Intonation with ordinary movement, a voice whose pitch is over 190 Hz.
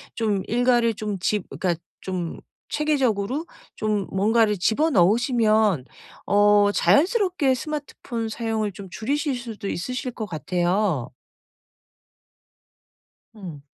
Yes: average, 4.1 semitones; high, 215 Hz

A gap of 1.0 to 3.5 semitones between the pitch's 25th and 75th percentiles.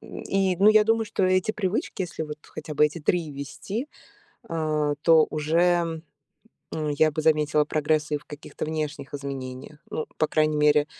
Yes: average, 2.8 semitones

